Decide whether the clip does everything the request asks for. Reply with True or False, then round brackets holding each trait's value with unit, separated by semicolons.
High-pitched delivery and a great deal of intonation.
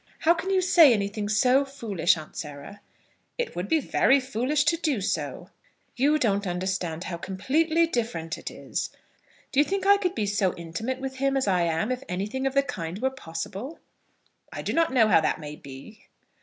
True (230 Hz; 7.2 semitones)